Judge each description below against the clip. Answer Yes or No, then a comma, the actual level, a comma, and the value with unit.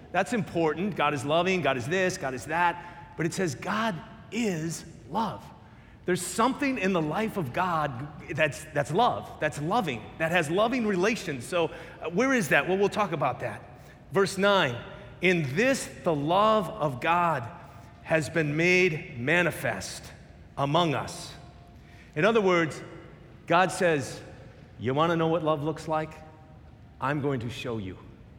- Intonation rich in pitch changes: No, average, 4.0 semitones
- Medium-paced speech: Yes, average, 155 wpm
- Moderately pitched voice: Yes, medium, 165 Hz